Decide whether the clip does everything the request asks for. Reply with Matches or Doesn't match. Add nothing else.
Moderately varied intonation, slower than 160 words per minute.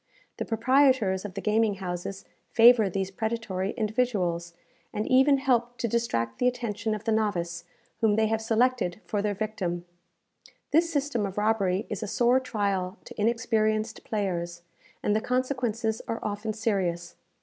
Matches